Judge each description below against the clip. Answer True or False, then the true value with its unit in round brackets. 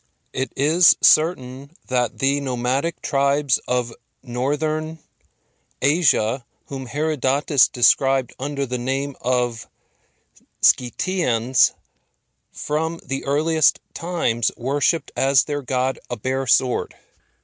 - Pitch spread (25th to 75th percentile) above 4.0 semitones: False (2.9 semitones)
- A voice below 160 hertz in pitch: True (135 Hz)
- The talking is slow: True (100 wpm)